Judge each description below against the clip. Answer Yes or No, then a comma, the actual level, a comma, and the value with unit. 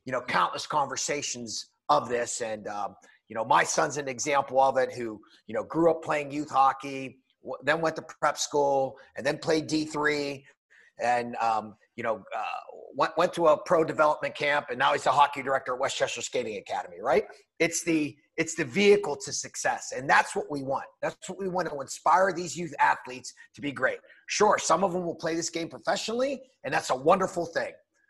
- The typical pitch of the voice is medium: Yes, medium, 155 Hz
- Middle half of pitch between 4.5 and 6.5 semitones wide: Yes, average, 4.8 semitones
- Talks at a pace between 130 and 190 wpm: No, fast, 205 wpm